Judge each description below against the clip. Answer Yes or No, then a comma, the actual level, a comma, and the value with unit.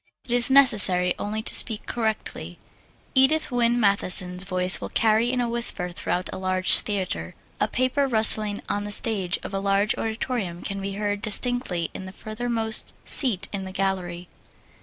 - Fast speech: No, average, 165 wpm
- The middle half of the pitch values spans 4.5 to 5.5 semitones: No, average, 4.0 semitones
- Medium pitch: No, high, 205 Hz